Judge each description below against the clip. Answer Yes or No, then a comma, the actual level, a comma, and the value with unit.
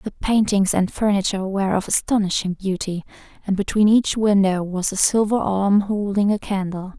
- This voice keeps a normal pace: Yes, average, 165 wpm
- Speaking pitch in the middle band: No, high, 200 Hz